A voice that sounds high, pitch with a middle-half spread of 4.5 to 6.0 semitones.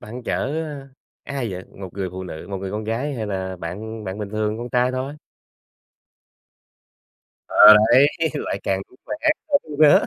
No: low, 110 Hz; average, 5.0 semitones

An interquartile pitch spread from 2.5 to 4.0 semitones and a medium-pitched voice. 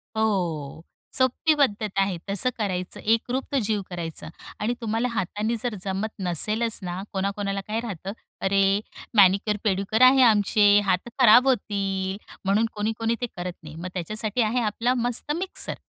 No: average, 3.0 semitones; high, 210 Hz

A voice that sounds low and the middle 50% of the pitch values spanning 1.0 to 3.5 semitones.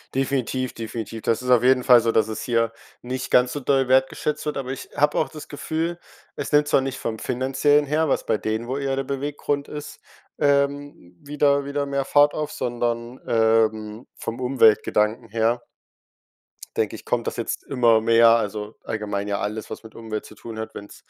No: low, 125 Hz; average, 4.0 semitones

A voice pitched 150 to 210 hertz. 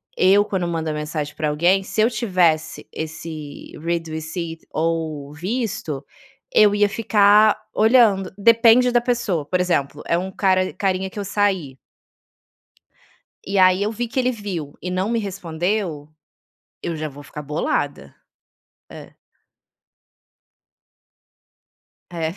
Yes: medium, 185 Hz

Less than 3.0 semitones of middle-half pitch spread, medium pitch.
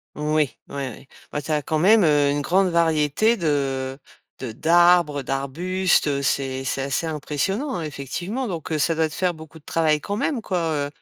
No: average, 3.8 semitones; medium, 155 Hz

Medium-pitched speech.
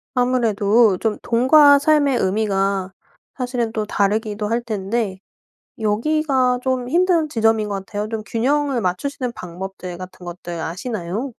No: high, 225 Hz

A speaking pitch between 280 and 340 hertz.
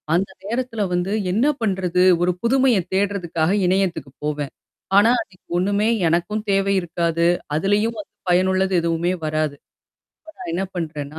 No: medium, 185 Hz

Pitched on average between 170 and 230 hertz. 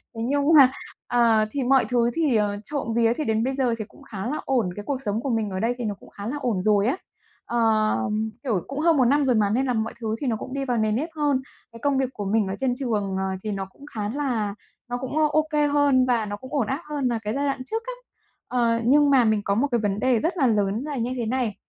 No: high, 240 Hz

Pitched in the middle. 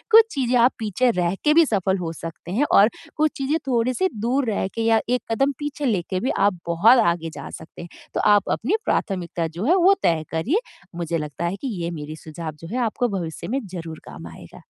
No: high, 200 Hz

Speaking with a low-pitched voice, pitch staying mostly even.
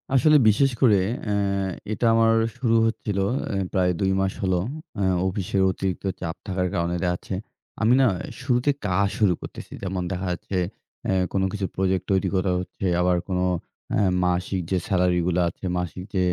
Yes: very low, 95 Hz; narrow, 2.2 semitones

